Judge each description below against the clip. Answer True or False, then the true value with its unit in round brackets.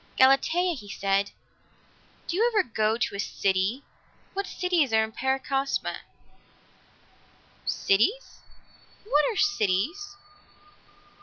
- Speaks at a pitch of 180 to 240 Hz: False (270 Hz)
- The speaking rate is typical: False (100 wpm)